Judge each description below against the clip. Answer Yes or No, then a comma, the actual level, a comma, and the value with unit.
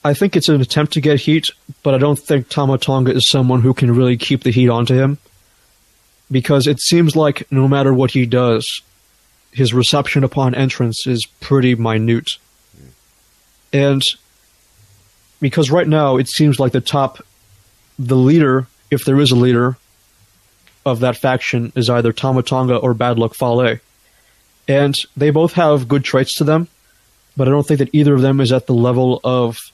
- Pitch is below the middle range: Yes, low, 130 Hz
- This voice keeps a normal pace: Yes, average, 175 wpm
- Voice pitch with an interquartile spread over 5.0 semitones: No, average, 3.0 semitones